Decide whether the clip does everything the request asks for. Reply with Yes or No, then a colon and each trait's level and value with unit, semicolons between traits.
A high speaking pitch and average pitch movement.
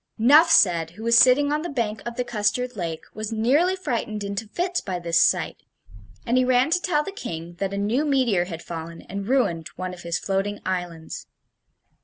No: high, 215 Hz; wide, 6.3 semitones